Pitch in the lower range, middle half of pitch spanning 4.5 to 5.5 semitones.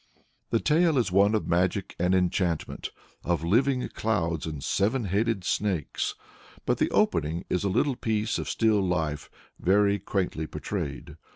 No: low, 100 Hz; average, 4.1 semitones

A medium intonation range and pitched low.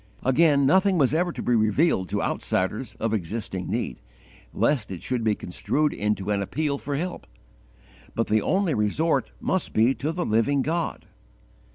No: wide, 6.8 semitones; low, 130 Hz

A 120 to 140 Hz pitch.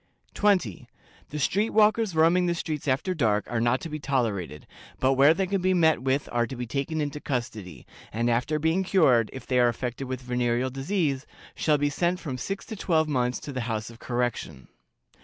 Yes: low, 135 Hz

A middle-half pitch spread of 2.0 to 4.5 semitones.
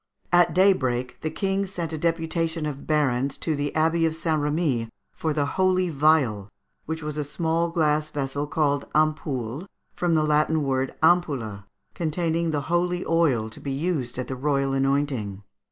Yes: average, 3.3 semitones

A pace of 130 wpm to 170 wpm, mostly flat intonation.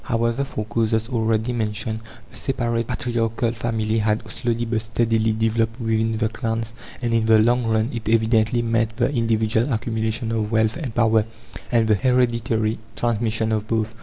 Yes: average, 165 wpm; narrow, 1.1 semitones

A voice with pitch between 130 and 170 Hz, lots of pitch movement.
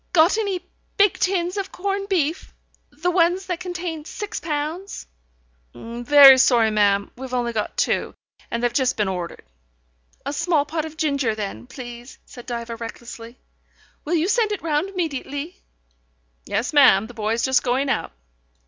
No: very high, 285 Hz; wide, 6.8 semitones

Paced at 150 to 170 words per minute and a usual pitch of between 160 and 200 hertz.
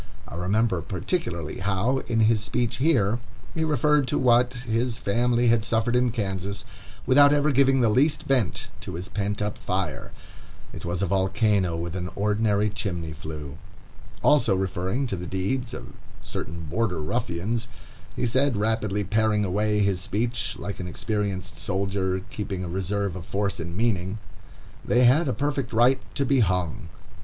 No: average, 160 wpm; low, 105 Hz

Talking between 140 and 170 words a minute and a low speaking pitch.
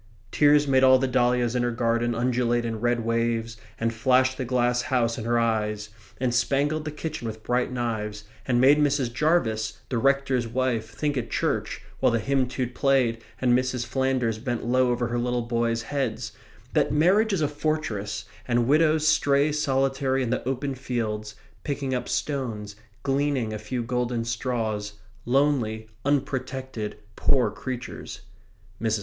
Yes: average, 160 wpm; low, 125 Hz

